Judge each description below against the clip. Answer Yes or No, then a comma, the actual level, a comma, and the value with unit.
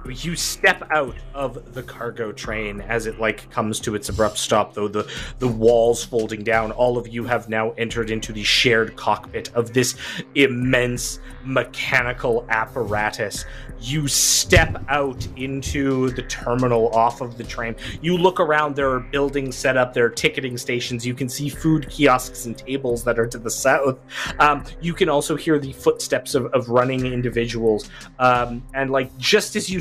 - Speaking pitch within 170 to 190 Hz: No, low, 125 Hz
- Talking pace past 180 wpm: No, average, 175 wpm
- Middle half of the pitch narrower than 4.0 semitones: Yes, average, 2.8 semitones